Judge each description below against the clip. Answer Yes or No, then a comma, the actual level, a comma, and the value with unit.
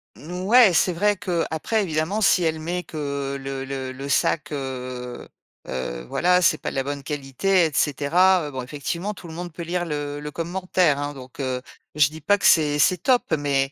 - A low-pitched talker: No, medium, 150 Hz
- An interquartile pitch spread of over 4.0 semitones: Yes, average, 4.5 semitones